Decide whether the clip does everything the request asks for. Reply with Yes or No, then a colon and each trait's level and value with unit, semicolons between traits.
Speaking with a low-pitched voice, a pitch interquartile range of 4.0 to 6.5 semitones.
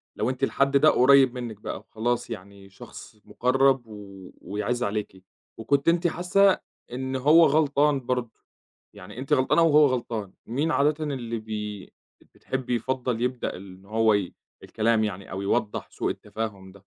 Yes: low, 120 Hz; average, 4.5 semitones